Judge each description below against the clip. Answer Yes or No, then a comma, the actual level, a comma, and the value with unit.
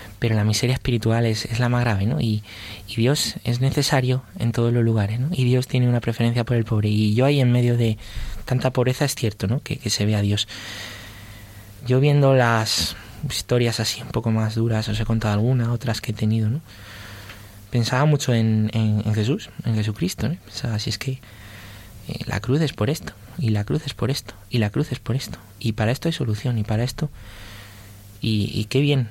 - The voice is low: Yes, low, 115 Hz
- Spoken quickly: Yes, fast, 220 wpm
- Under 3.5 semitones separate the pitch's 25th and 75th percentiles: Yes, average, 3.1 semitones